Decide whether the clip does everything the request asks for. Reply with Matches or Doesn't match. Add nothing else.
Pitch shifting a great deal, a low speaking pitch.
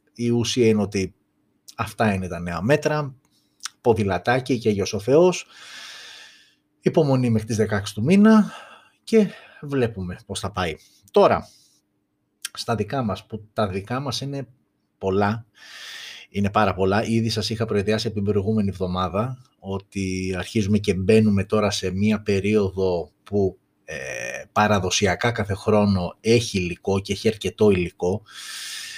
Doesn't match